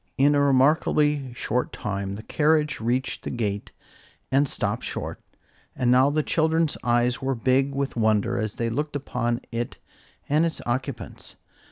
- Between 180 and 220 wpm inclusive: No, average, 155 wpm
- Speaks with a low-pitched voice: Yes, low, 130 Hz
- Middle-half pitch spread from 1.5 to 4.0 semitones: Yes, average, 3.5 semitones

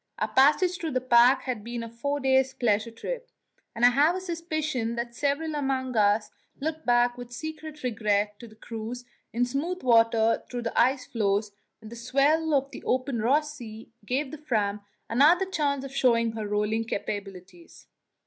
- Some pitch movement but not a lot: Yes, average, 4.1 semitones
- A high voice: Yes, high, 245 Hz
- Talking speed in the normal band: Yes, average, 175 wpm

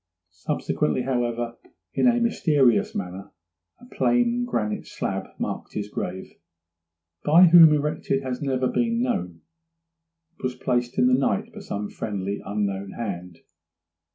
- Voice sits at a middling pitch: No, low, 125 Hz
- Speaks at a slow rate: Yes, slow, 130 wpm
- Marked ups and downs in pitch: Yes, wide, 8.6 semitones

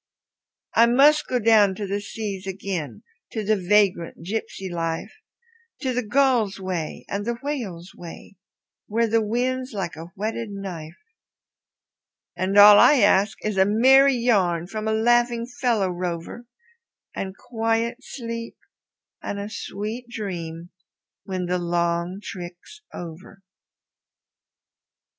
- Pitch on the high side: Yes, high, 205 Hz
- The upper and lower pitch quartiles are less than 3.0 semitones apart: No, average, 4.4 semitones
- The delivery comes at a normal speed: No, slow, 125 wpm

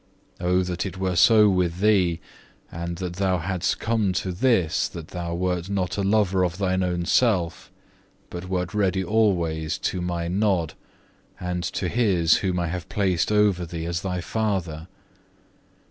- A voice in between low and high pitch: No, very low, 90 Hz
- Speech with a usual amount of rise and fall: No, narrow, 2.2 semitones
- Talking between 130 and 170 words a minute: Yes, average, 160 wpm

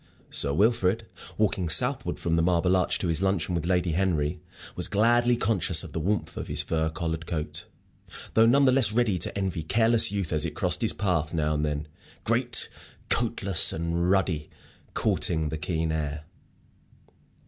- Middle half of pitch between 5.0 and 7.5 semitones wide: No, average, 4.3 semitones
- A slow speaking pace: No, average, 170 wpm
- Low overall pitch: Yes, very low, 90 Hz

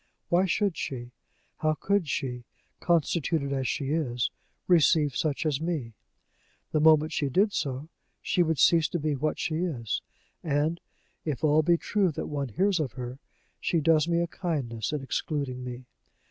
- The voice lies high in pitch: No, medium, 155 Hz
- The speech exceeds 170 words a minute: No, average, 165 wpm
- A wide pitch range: No, average, 3.9 semitones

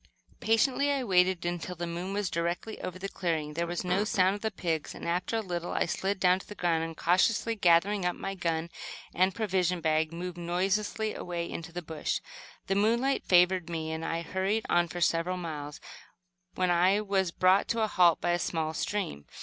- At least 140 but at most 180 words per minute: No, average, 200 wpm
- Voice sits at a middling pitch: Yes, medium, 180 Hz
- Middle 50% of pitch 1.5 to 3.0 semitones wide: Yes, narrow, 2.6 semitones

